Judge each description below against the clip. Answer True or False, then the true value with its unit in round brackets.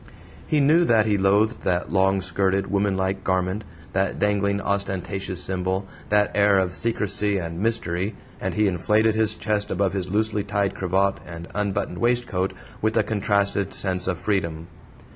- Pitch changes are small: True (1.9 semitones)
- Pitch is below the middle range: True (100 Hz)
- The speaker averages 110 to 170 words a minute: True (155 wpm)